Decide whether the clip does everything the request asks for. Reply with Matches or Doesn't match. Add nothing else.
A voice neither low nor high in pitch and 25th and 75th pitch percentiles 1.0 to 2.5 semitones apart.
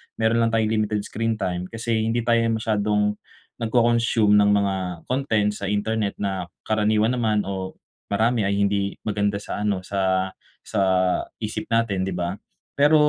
Doesn't match